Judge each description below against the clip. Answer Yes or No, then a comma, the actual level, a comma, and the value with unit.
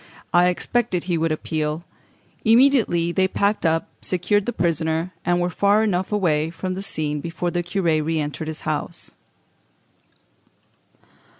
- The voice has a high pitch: No, medium, 175 Hz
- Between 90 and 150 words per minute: Yes, average, 140 wpm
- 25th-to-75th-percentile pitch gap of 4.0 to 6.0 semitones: No, average, 3.1 semitones